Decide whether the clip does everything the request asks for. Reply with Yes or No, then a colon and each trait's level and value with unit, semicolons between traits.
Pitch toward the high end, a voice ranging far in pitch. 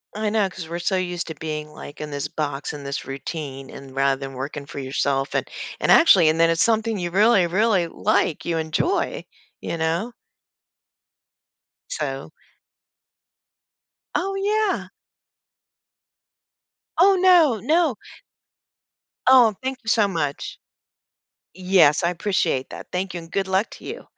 No: medium, 175 Hz; wide, 6.5 semitones